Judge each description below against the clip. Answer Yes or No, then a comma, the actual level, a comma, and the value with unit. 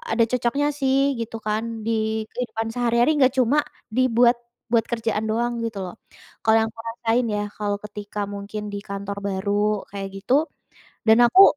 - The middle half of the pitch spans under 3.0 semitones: Yes, narrow, 2.5 semitones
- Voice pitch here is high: Yes, high, 225 Hz